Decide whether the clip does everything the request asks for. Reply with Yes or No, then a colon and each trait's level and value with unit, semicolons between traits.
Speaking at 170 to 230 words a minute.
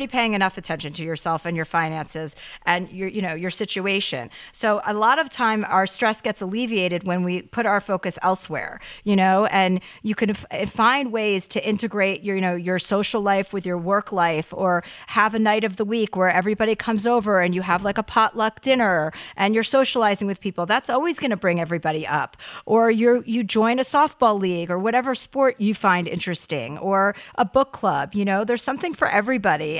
Yes: fast, 205 wpm